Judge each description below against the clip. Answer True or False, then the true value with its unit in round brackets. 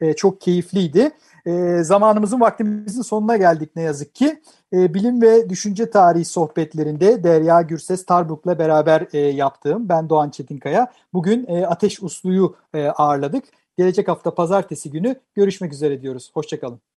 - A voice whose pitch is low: False (175 Hz)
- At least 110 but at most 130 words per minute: True (120 wpm)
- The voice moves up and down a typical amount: True (4.8 semitones)